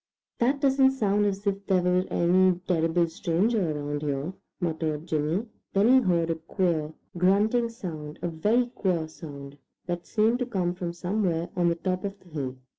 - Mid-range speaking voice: Yes, medium, 180 Hz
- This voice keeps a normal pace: Yes, average, 175 wpm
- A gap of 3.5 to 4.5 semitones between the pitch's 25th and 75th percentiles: Yes, average, 4.0 semitones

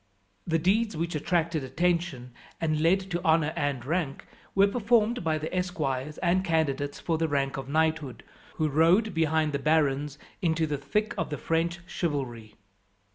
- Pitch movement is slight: No, average, 3.4 semitones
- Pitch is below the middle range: No, medium, 160 Hz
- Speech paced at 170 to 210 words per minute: No, average, 160 wpm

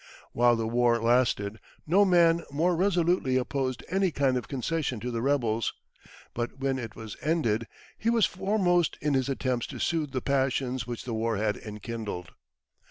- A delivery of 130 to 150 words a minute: No, average, 165 wpm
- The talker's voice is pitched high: No, low, 130 Hz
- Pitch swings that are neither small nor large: No, wide, 5.9 semitones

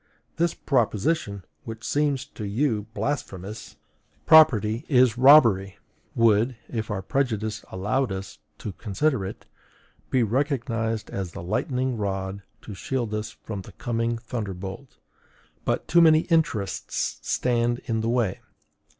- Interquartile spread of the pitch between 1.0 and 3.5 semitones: No, average, 4.4 semitones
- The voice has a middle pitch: No, low, 115 Hz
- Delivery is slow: Yes, slow, 125 wpm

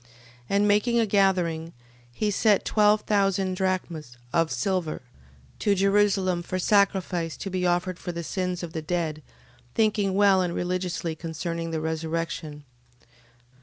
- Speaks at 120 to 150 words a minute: Yes, average, 140 wpm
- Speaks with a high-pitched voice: No, medium, 180 Hz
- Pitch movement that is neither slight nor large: Yes, average, 3.1 semitones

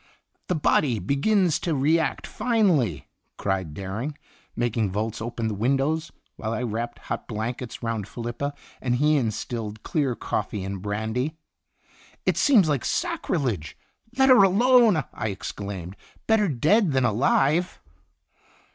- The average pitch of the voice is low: Yes, low, 125 Hz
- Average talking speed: No, slow, 130 wpm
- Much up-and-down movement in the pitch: Yes, wide, 6.7 semitones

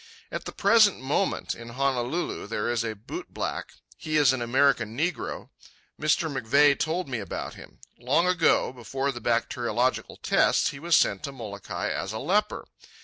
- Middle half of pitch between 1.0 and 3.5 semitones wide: No, average, 4.8 semitones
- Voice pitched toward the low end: Yes, low, 130 Hz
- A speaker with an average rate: Yes, average, 160 wpm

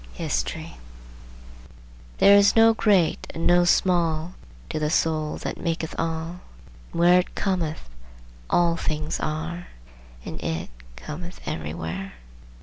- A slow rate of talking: Yes, slow, 120 wpm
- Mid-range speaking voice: Yes, medium, 165 Hz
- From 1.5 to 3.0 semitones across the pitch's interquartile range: Yes, narrow, 2.5 semitones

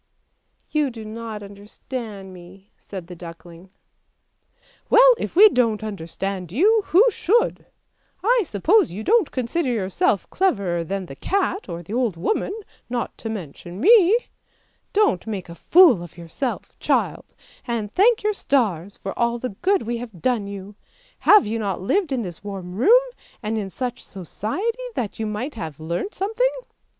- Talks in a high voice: Yes, high, 220 Hz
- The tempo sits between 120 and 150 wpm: No, average, 165 wpm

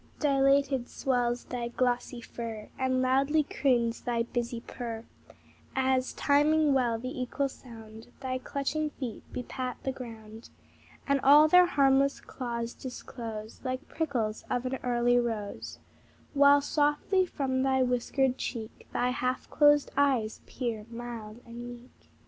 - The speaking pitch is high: Yes, very high, 255 Hz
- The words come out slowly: Yes, slow, 130 wpm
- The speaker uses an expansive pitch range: No, narrow, 2.6 semitones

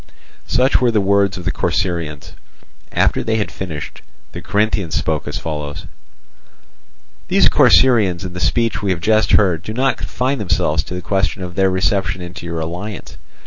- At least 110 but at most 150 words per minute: No, average, 170 wpm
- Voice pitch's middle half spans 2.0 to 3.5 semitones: No, average, 3.9 semitones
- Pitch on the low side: Yes, very low, 95 Hz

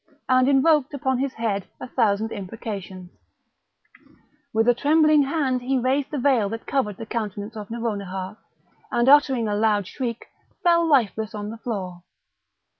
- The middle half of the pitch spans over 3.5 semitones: Yes, average, 4.5 semitones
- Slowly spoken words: No, average, 150 wpm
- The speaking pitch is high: Yes, high, 230 Hz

